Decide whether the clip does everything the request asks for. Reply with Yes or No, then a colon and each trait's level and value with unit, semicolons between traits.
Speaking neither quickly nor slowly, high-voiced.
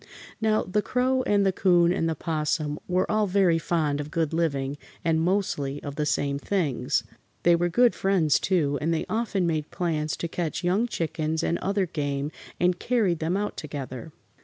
No: average, 185 wpm; medium, 165 Hz